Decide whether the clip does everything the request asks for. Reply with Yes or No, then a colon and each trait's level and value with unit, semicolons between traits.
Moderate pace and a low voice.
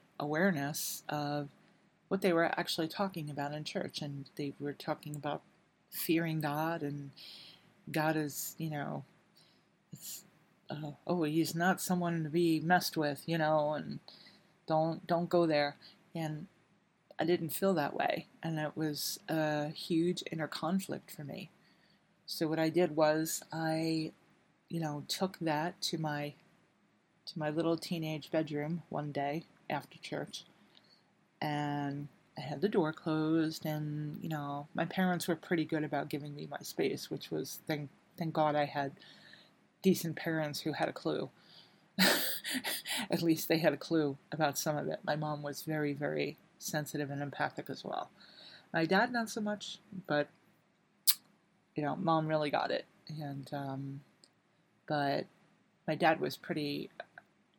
No: average, 150 wpm; medium, 160 Hz